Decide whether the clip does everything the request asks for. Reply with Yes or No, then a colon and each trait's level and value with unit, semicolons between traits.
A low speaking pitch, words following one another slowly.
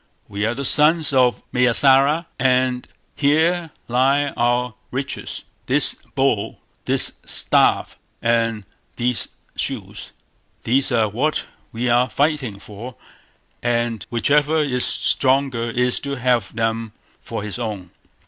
Yes: low, 125 Hz; slow, 120 wpm